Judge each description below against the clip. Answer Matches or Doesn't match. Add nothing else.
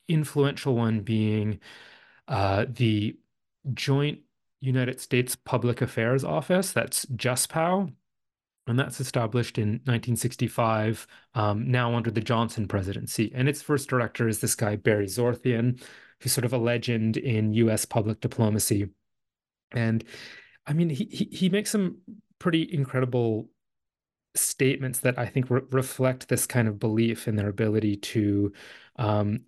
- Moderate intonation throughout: Matches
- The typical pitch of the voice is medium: Doesn't match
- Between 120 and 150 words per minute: Matches